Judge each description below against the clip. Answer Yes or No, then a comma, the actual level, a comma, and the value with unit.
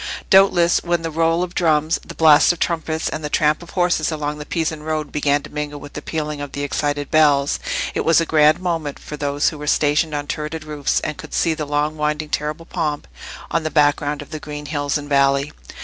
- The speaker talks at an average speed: No, fast, 225 wpm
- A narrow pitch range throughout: Yes, narrow, 1.7 semitones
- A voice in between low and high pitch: Yes, medium, 150 Hz